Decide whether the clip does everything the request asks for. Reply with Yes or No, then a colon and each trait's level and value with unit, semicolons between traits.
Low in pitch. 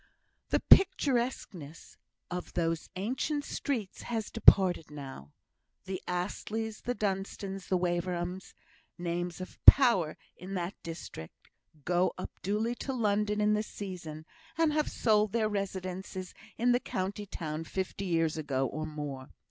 No: medium, 185 Hz